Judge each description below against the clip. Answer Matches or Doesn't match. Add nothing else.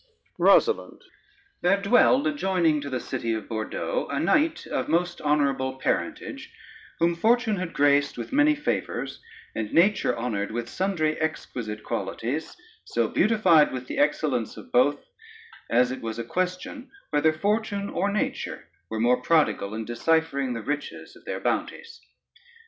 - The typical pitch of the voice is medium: Matches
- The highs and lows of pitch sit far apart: Matches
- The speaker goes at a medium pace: Matches